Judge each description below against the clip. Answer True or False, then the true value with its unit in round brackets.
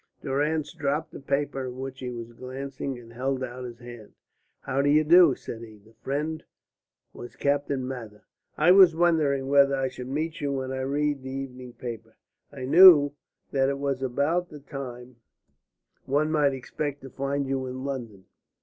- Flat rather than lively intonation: True (2.3 semitones)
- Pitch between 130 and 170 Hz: True (135 Hz)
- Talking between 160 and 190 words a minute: True (175 wpm)